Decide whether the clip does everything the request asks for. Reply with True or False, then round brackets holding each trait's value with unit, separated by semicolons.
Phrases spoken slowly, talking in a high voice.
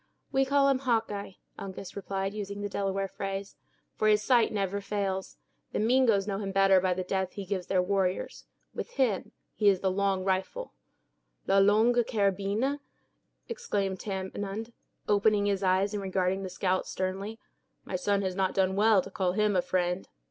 False (170 wpm; 195 Hz)